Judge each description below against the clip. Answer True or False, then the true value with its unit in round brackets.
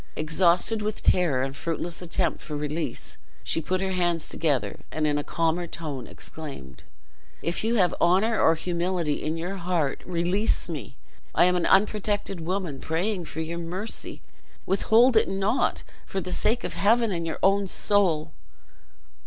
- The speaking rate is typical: True (160 wpm)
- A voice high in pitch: False (175 Hz)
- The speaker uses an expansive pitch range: False (3.3 semitones)